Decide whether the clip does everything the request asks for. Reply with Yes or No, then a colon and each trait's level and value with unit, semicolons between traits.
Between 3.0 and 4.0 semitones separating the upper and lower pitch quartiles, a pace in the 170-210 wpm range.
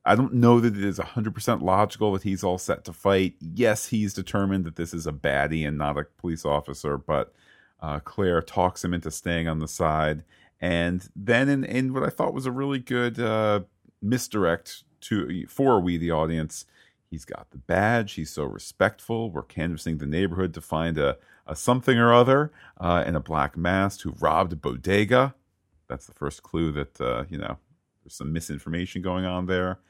No: average, 4.8 semitones; average, 195 wpm